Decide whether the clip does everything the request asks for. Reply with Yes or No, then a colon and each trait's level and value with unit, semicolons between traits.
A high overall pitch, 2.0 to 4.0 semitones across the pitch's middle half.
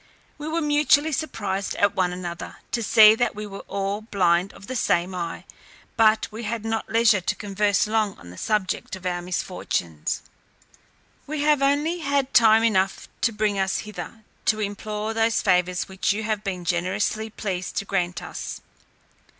Yes: high, 210 Hz; average, 3.2 semitones